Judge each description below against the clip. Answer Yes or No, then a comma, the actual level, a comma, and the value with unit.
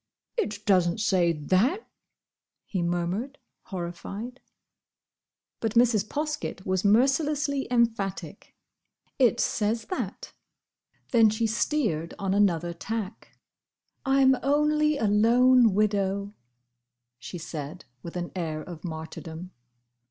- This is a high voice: Yes, high, 210 Hz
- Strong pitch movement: Yes, wide, 6.0 semitones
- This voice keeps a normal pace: No, slow, 105 wpm